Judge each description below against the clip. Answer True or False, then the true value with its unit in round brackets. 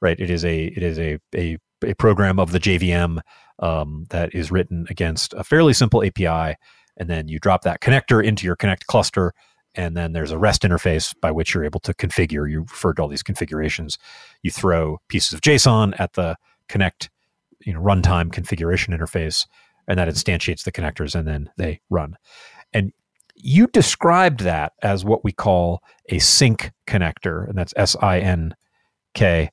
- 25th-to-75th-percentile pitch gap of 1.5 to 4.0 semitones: True (3.4 semitones)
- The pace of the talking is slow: False (180 wpm)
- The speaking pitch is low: True (90 Hz)